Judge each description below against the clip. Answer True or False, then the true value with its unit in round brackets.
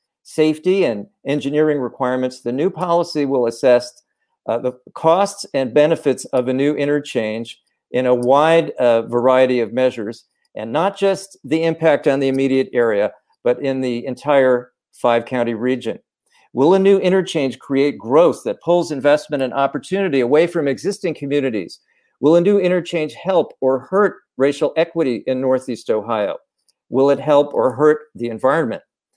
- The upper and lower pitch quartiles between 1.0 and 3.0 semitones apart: False (4.1 semitones)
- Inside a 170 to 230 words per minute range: False (155 wpm)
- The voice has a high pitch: False (140 Hz)